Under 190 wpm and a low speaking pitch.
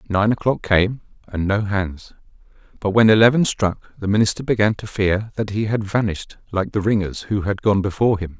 No: average, 195 wpm; low, 105 Hz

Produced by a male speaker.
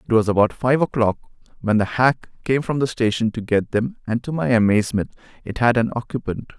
Yes: male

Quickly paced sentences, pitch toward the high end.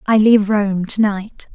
No: average, 195 wpm; high, 205 Hz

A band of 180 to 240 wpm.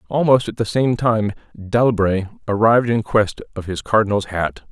No: average, 165 wpm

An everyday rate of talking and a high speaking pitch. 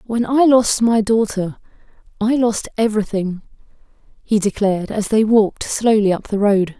Yes: average, 150 wpm; high, 215 Hz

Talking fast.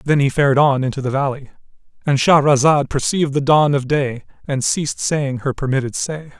No: average, 180 wpm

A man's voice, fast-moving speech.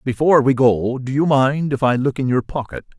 Yes: male; fast, 240 wpm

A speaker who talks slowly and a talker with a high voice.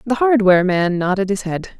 No: average, 200 wpm; high, 200 Hz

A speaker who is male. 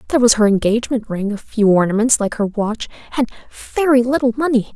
No: female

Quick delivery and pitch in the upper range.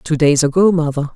No: fast, 210 wpm; medium, 155 Hz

